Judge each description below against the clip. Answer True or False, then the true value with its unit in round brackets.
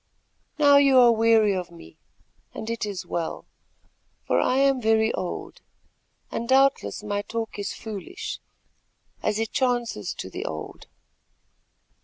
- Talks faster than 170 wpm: False (135 wpm)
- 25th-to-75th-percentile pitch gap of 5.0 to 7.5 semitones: False (3.7 semitones)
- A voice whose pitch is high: True (225 Hz)